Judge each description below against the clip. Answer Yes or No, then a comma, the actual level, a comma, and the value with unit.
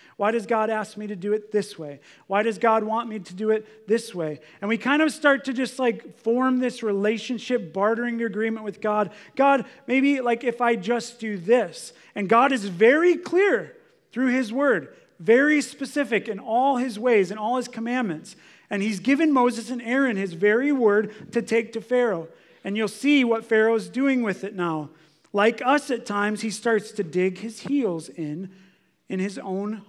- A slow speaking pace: No, average, 195 wpm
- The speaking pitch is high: Yes, high, 225 Hz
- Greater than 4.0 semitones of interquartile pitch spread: No, average, 3.4 semitones